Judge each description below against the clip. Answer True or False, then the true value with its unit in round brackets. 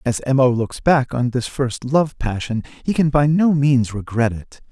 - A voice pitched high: False (130 Hz)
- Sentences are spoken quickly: True (215 wpm)